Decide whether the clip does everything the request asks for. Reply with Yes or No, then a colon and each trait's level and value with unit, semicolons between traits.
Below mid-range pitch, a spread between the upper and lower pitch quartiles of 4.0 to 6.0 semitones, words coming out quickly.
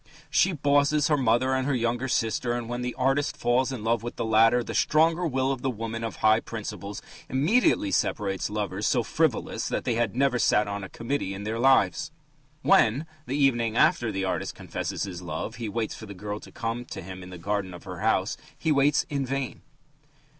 Yes: low, 120 Hz; average, 4.3 semitones; fast, 210 wpm